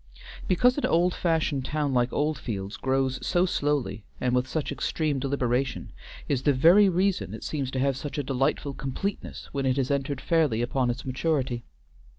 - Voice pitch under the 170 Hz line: Yes, medium, 140 Hz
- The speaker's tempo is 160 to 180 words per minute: Yes, average, 170 wpm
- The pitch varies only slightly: No, average, 3.5 semitones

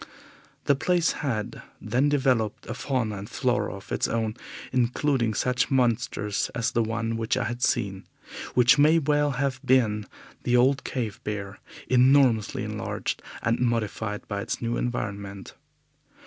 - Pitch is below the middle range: Yes, low, 120 Hz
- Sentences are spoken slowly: No, average, 145 wpm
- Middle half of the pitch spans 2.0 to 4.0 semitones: Yes, average, 3.6 semitones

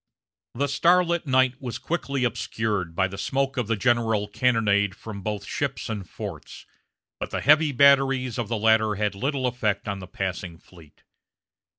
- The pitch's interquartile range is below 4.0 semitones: No, average, 4.7 semitones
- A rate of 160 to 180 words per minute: Yes, average, 165 wpm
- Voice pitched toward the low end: Yes, low, 115 Hz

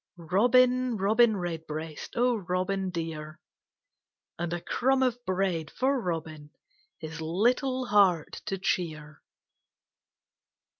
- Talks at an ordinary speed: No, slow, 100 wpm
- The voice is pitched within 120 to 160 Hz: No, medium, 185 Hz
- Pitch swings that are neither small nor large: No, wide, 6.7 semitones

